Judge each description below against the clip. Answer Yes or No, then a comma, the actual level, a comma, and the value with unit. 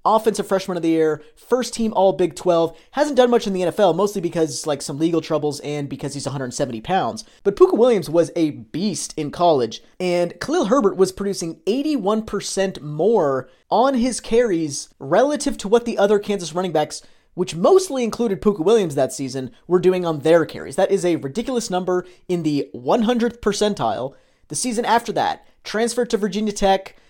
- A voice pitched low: No, high, 190 Hz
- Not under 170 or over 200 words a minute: Yes, average, 180 wpm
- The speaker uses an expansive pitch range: Yes, wide, 5.8 semitones